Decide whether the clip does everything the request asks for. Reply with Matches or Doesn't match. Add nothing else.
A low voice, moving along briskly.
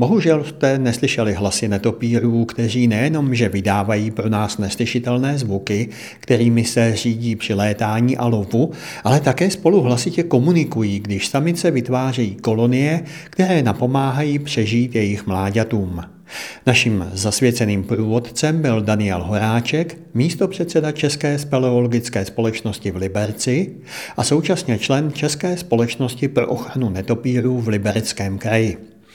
Doesn't match